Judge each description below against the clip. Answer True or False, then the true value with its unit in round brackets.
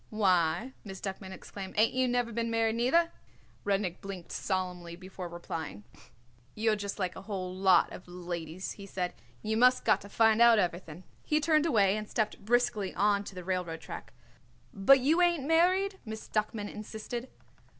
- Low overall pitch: False (205 Hz)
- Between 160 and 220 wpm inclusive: True (170 wpm)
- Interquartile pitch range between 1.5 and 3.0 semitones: False (4.2 semitones)